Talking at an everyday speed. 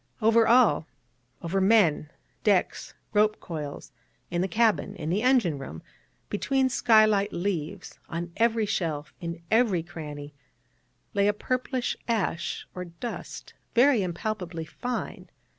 No: slow, 125 wpm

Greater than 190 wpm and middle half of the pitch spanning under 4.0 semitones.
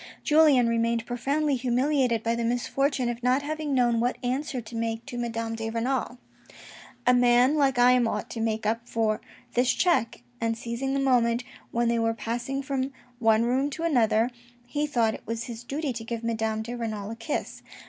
Yes: average, 200 wpm; narrow, 2.6 semitones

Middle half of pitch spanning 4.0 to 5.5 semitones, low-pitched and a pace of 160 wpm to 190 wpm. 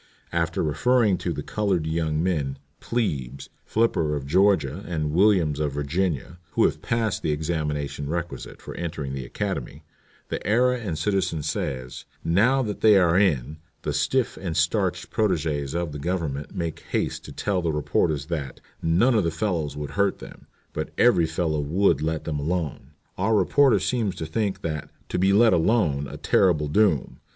Yes: average, 4.9 semitones; very low, 85 Hz; average, 170 wpm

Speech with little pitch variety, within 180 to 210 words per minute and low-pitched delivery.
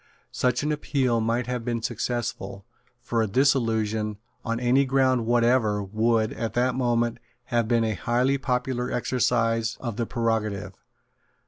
No: narrow, 2.0 semitones; average, 140 wpm; low, 120 Hz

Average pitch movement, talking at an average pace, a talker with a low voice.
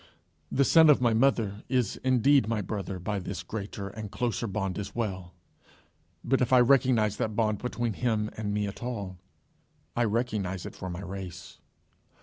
Yes: average, 3.7 semitones; average, 170 wpm; low, 110 Hz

